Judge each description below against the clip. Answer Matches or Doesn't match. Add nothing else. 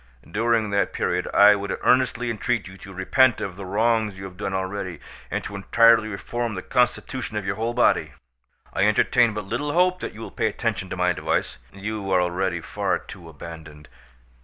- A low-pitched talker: Matches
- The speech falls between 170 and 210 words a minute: Matches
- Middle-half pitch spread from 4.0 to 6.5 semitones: Doesn't match